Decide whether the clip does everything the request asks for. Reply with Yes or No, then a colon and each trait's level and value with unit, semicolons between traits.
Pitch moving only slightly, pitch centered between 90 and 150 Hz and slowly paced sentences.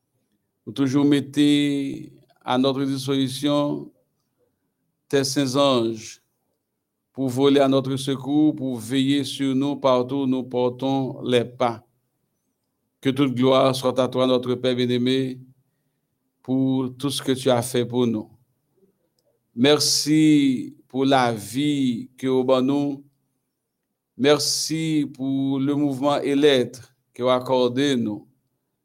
Yes: narrow, 1.9 semitones; low, 135 Hz; slow, 125 wpm